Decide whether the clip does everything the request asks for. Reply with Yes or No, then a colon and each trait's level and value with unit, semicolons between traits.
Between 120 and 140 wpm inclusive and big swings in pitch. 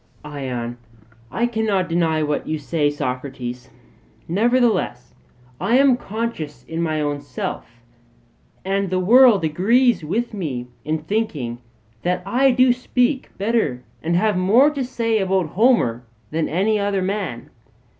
Yes: slow, 135 wpm; wide, 7.3 semitones